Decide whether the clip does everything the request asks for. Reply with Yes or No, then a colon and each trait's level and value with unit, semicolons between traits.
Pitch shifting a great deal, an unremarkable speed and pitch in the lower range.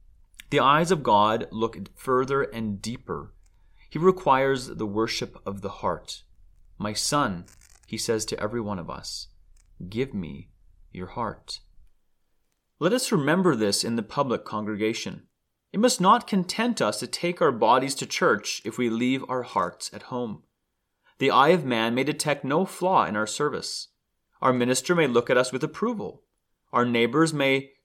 Yes: wide, 6.2 semitones; average, 165 wpm; low, 125 Hz